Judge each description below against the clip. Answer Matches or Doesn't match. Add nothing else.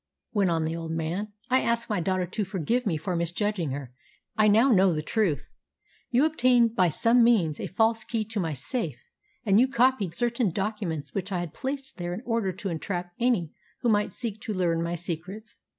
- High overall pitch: Matches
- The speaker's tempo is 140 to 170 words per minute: Doesn't match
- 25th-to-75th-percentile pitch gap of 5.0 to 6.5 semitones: Matches